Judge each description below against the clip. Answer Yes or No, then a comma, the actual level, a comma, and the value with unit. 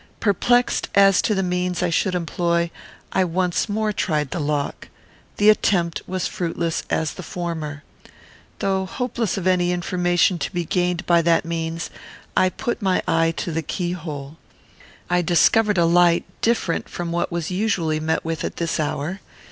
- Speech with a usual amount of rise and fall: No, narrow, 2.2 semitones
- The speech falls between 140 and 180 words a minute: Yes, average, 165 wpm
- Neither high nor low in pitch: Yes, medium, 175 Hz